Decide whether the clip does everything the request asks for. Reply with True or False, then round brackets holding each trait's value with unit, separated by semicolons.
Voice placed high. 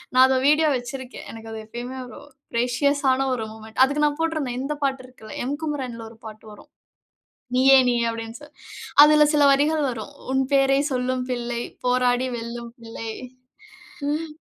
True (255 Hz)